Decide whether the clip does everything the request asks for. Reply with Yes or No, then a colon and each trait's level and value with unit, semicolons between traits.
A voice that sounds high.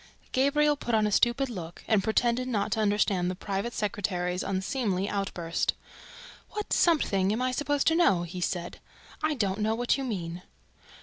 Yes: high, 210 Hz